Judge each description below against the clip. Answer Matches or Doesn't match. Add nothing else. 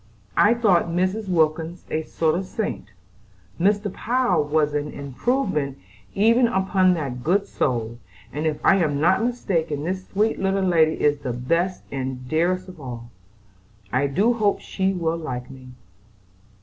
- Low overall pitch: Doesn't match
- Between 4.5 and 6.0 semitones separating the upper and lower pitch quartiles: Matches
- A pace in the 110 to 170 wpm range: Matches